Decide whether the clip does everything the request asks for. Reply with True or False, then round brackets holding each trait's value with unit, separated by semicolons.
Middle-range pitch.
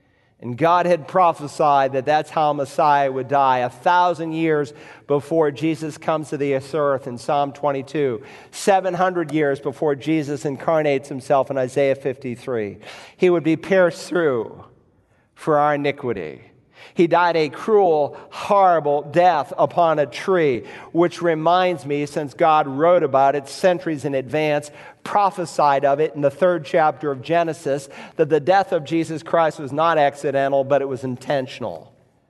True (150 Hz)